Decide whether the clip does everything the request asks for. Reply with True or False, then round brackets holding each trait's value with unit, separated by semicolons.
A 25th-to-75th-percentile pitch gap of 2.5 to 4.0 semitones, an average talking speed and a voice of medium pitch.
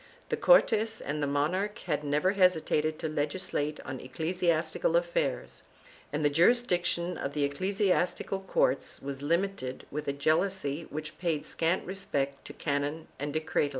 False (4.5 semitones; 150 wpm; 160 Hz)